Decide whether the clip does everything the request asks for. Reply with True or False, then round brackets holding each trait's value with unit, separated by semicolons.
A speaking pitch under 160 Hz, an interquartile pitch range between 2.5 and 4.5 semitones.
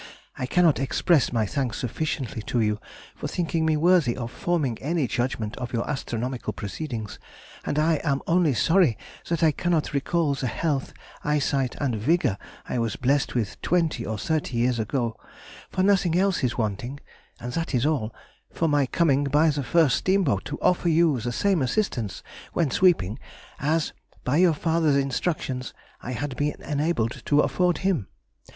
False (140 Hz; 5.1 semitones)